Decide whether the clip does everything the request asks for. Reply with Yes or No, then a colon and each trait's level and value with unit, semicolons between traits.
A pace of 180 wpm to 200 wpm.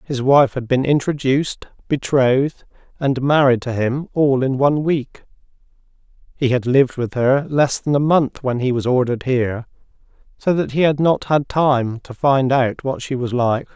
Yes: average, 185 wpm